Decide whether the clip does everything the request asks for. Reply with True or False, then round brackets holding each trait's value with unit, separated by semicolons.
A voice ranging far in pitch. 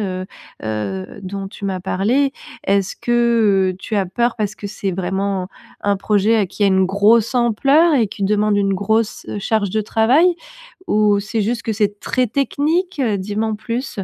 False (3.0 semitones)